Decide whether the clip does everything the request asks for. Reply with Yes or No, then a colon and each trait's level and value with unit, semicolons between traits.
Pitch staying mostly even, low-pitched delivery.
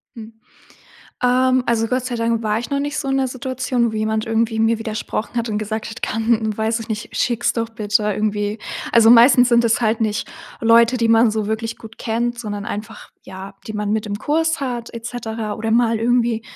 No: narrow, 1.7 semitones; high, 225 Hz